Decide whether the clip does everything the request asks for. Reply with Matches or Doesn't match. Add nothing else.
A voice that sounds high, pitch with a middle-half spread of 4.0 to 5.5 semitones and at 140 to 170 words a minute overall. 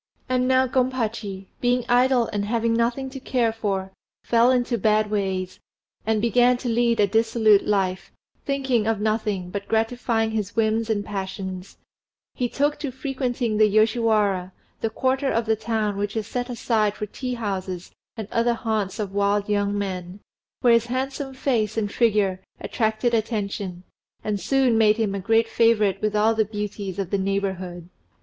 Doesn't match